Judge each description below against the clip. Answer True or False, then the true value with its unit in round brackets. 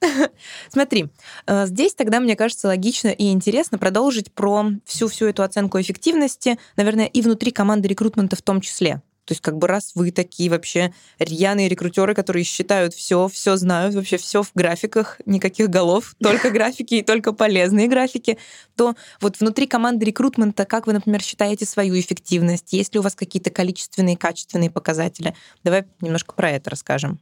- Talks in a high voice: True (200 Hz)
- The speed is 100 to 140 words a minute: False (160 wpm)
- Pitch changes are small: False (3.3 semitones)